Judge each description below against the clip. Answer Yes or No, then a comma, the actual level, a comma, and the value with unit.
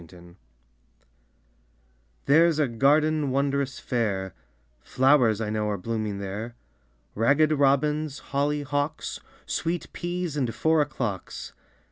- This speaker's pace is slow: Yes, slow, 110 wpm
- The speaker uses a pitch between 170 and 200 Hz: No, low, 135 Hz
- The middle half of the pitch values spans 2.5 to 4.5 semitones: No, wide, 5.4 semitones